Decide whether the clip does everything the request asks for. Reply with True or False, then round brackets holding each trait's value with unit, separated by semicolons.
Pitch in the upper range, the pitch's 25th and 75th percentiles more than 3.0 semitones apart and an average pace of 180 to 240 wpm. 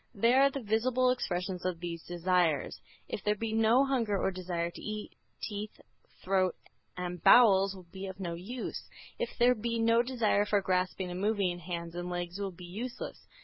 True (195 Hz; 4.2 semitones; 185 wpm)